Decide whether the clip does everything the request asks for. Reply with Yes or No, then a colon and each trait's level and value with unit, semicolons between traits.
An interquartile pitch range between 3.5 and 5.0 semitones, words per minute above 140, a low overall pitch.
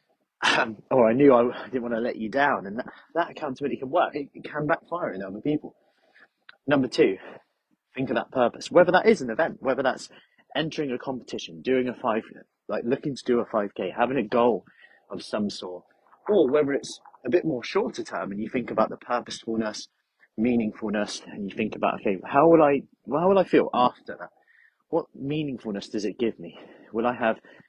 Yes: average, 4.4 semitones; average, 200 wpm; low, 120 Hz